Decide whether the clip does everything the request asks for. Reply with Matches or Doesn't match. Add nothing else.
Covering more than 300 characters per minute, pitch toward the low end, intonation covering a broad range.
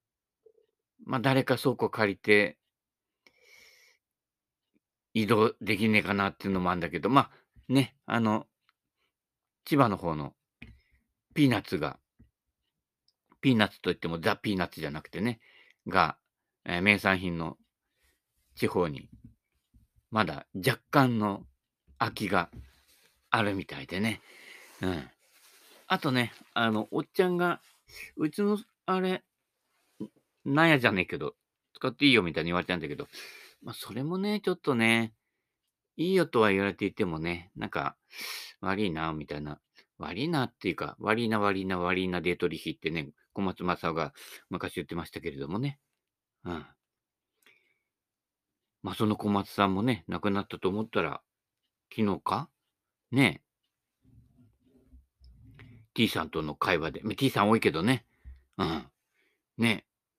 Doesn't match